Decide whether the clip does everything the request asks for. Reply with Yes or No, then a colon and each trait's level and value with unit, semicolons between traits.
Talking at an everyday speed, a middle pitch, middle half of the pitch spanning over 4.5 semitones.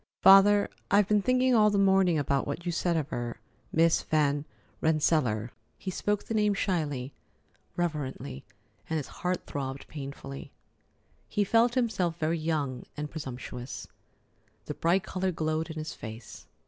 Yes: average, 145 wpm; medium, 160 Hz; average, 5.3 semitones